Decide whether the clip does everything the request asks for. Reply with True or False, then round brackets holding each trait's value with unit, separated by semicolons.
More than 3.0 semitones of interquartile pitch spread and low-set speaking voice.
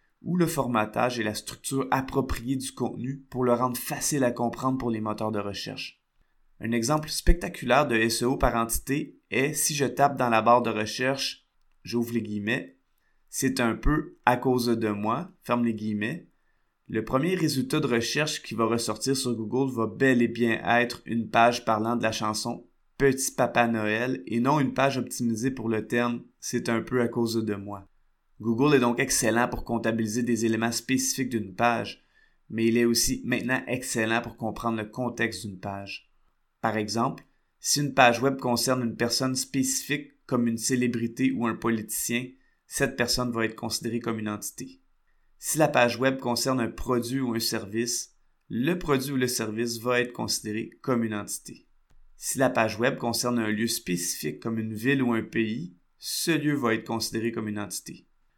False (2.5 semitones; 120 Hz)